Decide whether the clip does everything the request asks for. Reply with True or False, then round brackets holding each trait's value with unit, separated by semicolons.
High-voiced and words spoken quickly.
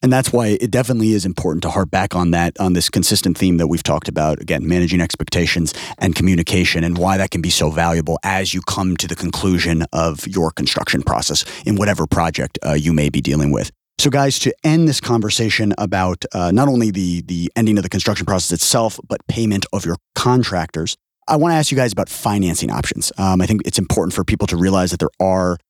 False (95 Hz; 220 wpm)